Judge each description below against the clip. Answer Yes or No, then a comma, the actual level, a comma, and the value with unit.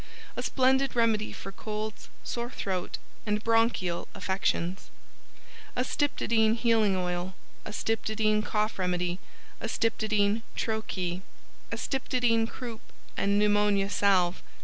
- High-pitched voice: Yes, high, 215 Hz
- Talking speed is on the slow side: Yes, slow, 100 wpm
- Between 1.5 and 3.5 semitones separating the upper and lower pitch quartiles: Yes, average, 2.9 semitones